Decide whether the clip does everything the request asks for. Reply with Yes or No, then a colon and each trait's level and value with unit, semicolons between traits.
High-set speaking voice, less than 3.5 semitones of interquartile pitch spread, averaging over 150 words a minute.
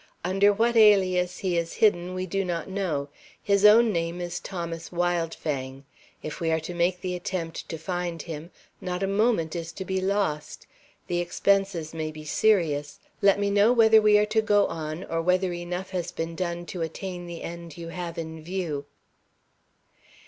No: medium, 175 Hz; average, 2.9 semitones; average, 180 wpm